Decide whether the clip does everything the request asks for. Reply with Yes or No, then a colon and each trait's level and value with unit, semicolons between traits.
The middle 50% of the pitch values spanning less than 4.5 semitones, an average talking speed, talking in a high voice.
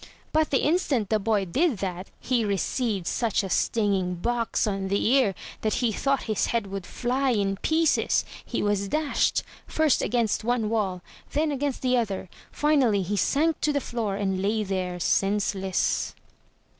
No: average, 5.0 semitones; average, 170 wpm; high, 220 Hz